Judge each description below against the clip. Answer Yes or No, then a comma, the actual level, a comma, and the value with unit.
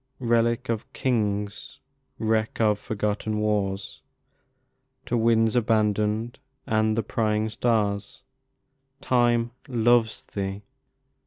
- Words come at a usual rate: No, slow, 95 wpm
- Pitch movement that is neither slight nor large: No, narrow, 1.8 semitones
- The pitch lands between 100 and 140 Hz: Yes, low, 110 Hz